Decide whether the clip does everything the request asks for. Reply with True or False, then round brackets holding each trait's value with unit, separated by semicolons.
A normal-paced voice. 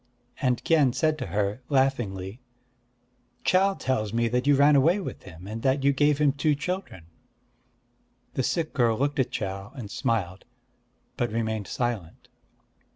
True (155 wpm)